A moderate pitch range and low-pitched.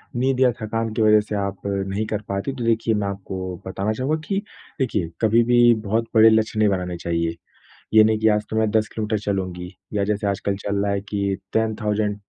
No: narrow, 2.0 semitones; low, 105 Hz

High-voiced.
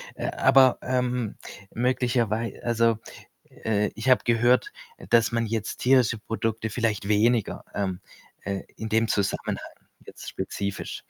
No: low, 115 Hz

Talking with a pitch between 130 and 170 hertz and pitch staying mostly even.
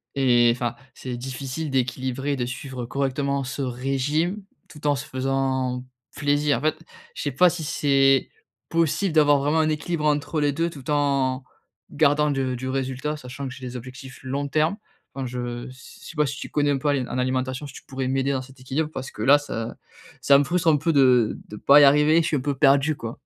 Yes: low, 135 Hz; narrow, 2.3 semitones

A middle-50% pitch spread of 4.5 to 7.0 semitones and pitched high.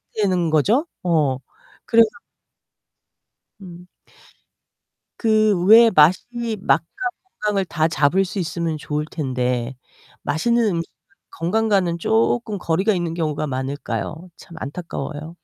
No: average, 5.1 semitones; medium, 170 Hz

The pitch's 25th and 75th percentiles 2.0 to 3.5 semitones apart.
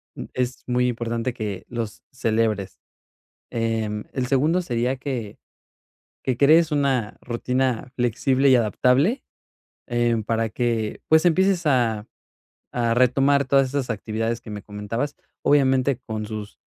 Yes: average, 3.2 semitones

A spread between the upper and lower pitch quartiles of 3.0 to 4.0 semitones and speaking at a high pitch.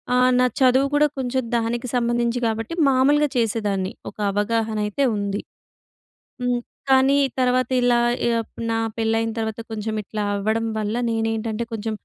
No: narrow, 2.4 semitones; high, 230 Hz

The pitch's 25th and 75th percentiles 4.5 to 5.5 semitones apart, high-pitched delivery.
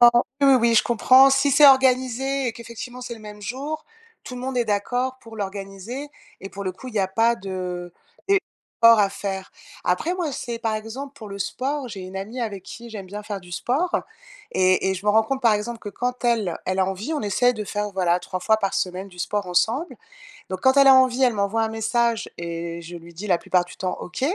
Yes: average, 4.8 semitones; high, 220 Hz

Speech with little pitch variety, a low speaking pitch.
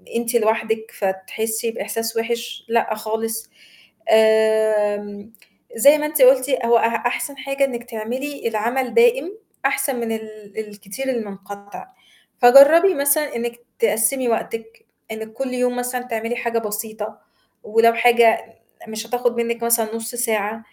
No: narrow, 2.3 semitones; high, 230 Hz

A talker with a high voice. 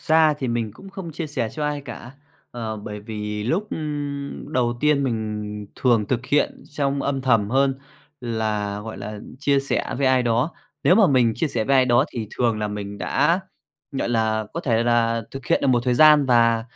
No: low, 120 Hz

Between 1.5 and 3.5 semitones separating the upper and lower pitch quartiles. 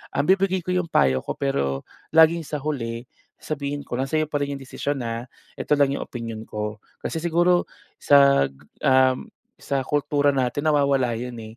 No: average, 4.1 semitones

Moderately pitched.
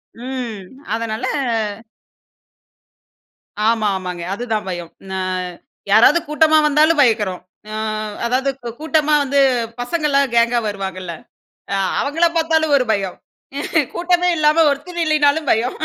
No: very high, 255 Hz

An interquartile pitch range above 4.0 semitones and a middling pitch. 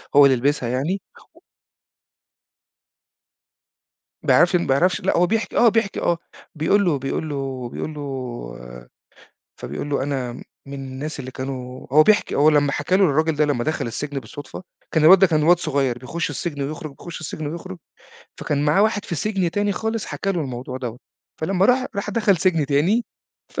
Yes: average, 5.0 semitones; medium, 150 Hz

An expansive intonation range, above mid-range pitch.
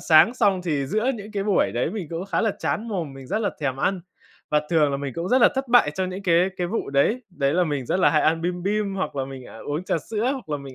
No: wide, 6.1 semitones; medium, 180 Hz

